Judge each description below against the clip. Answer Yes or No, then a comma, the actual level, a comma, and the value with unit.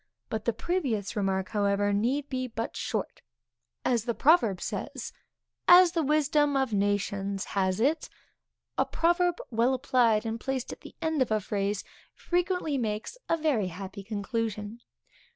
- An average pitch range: No, wide, 6.2 semitones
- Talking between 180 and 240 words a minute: No, average, 150 wpm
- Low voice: No, high, 230 Hz